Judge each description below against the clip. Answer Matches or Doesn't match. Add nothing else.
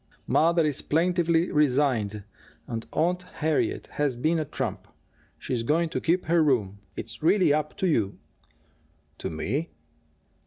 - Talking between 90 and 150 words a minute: Matches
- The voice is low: Doesn't match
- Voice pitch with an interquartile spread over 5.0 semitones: Matches